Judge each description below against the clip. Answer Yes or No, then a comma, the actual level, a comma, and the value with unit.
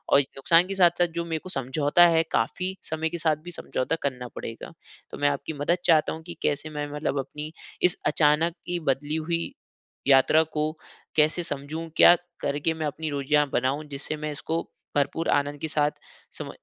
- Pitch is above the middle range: No, medium, 155 Hz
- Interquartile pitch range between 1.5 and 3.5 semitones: Yes, narrow, 2.5 semitones